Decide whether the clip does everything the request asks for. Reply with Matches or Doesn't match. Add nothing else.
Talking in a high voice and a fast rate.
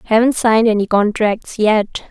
Doesn't match